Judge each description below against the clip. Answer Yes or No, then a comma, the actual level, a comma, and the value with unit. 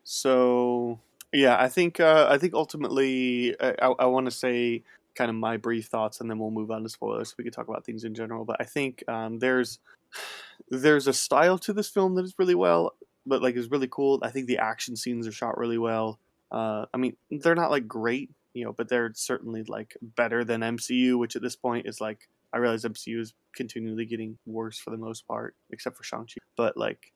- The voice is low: Yes, low, 120 Hz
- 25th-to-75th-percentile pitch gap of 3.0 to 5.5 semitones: No, narrow, 2.4 semitones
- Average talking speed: No, fast, 225 wpm